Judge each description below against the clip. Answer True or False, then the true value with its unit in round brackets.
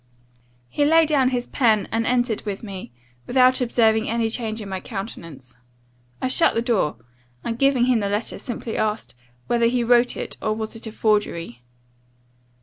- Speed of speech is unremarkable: True (170 wpm)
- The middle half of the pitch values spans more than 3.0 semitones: False (2.7 semitones)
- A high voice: True (225 Hz)